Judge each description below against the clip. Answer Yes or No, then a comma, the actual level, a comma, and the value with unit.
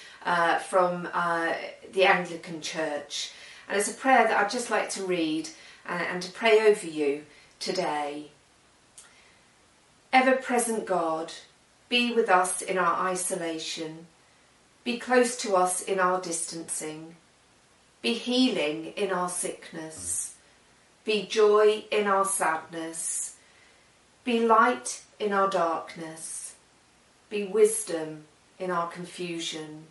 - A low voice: No, medium, 180 Hz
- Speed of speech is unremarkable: No, slow, 120 wpm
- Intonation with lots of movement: No, average, 4.4 semitones